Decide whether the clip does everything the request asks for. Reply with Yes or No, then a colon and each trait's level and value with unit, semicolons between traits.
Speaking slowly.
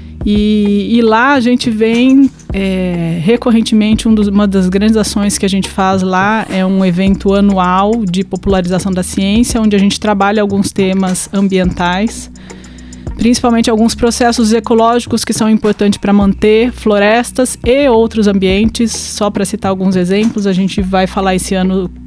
No: average, 160 wpm